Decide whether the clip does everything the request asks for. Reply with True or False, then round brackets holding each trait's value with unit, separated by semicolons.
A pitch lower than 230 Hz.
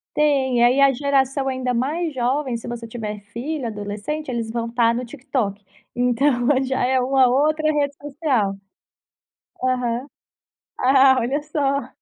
False (255 Hz)